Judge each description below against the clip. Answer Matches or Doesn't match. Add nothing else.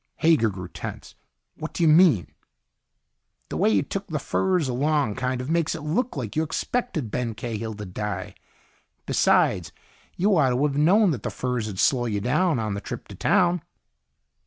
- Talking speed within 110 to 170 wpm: Doesn't match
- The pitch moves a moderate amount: Doesn't match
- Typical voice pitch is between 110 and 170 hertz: Matches